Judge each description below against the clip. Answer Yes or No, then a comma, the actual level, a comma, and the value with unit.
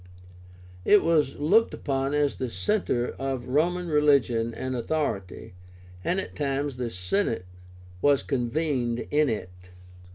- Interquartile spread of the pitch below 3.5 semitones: No, average, 4.2 semitones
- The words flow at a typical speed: No, slow, 125 wpm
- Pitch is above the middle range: No, low, 135 Hz